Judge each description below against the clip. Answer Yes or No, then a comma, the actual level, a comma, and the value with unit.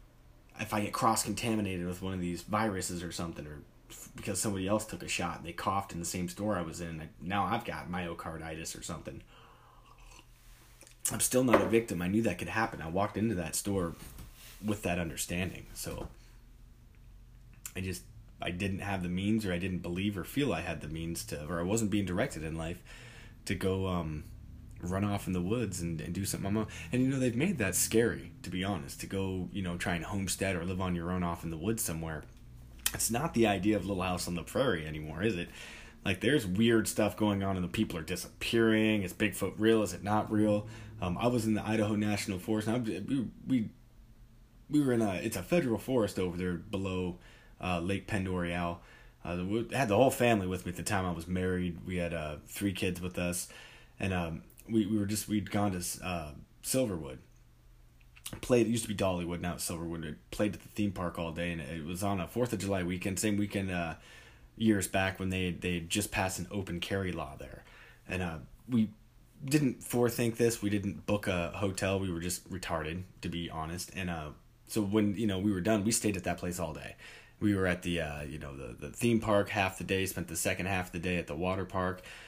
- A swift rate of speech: Yes, fast, 225 wpm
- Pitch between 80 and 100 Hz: Yes, very low, 95 Hz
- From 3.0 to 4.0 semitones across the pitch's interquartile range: Yes, average, 3.7 semitones